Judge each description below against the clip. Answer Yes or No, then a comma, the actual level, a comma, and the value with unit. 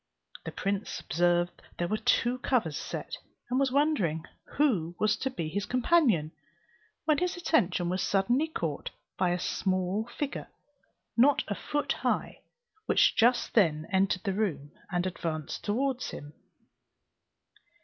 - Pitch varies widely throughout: Yes, wide, 6.6 semitones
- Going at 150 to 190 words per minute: No, average, 140 wpm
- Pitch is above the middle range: Yes, high, 200 Hz